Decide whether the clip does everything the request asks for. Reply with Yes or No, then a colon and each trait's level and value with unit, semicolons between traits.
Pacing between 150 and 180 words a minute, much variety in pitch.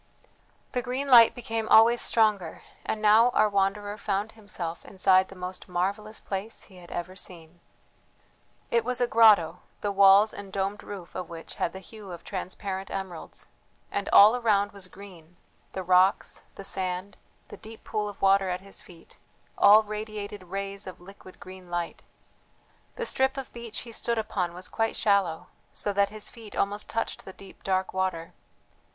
No: average, 170 wpm; narrow, 2.6 semitones